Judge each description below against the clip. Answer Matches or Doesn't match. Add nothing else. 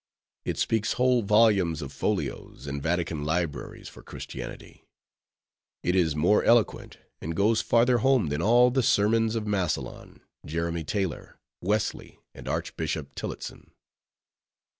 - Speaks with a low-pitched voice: Matches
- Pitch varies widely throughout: Matches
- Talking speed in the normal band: Doesn't match